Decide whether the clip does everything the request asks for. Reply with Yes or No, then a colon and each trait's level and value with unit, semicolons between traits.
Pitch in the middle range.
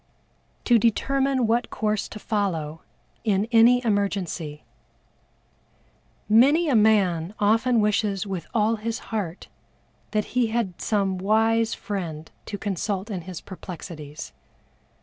No: high, 210 Hz